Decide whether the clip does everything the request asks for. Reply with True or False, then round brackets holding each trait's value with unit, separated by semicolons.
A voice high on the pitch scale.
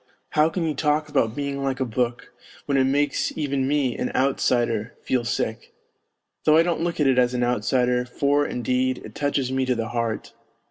False (130 Hz)